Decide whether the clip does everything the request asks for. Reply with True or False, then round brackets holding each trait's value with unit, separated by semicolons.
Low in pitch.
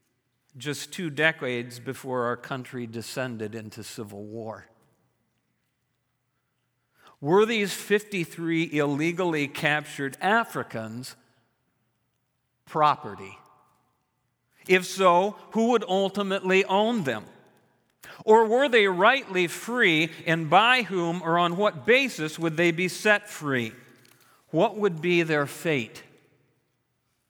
False (150 Hz)